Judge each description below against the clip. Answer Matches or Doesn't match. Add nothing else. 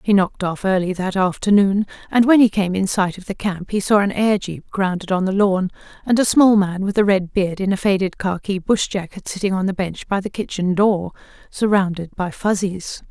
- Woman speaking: Matches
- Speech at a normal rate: Doesn't match